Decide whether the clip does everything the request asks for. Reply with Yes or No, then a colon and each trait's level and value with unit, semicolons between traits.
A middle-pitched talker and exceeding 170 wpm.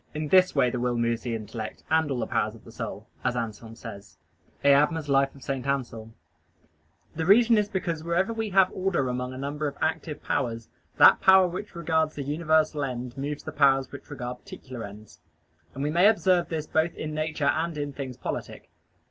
Yes: medium, 145 Hz; average, 190 wpm